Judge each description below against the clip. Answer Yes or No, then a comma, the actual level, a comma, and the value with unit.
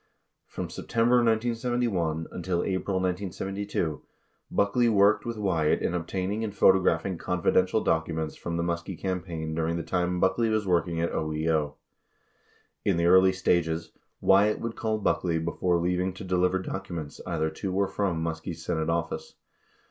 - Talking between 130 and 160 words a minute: Yes, average, 145 wpm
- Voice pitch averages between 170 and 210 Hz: No, very low, 90 Hz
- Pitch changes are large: No, average, 3.1 semitones